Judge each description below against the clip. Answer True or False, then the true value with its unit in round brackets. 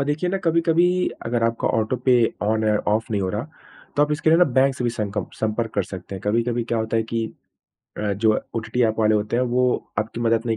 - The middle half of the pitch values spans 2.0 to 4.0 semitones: True (2.8 semitones)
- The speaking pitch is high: False (115 Hz)